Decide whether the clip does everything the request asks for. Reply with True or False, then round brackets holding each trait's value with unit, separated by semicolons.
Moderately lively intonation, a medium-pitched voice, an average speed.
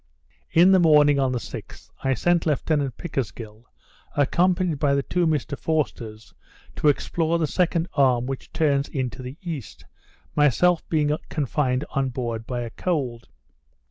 True (4.1 semitones; 145 Hz; 150 wpm)